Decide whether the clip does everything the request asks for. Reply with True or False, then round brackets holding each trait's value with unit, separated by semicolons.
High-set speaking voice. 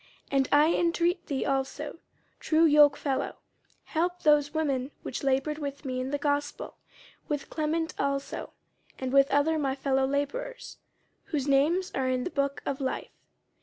True (285 Hz)